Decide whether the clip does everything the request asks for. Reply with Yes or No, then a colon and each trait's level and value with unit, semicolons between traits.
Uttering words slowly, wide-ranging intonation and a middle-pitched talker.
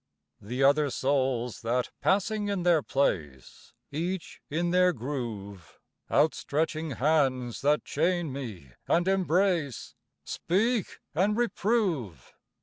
Yes: slow, 110 wpm; wide, 6.4 semitones; medium, 150 Hz